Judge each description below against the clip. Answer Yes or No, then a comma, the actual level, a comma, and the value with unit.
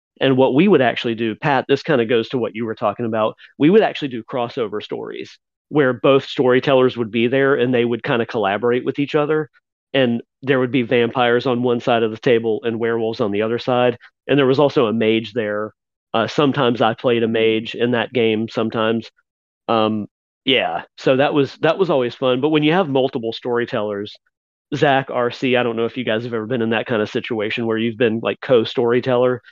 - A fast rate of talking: Yes, fast, 220 wpm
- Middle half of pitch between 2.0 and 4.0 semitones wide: Yes, narrow, 2.6 semitones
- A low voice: Yes, low, 120 Hz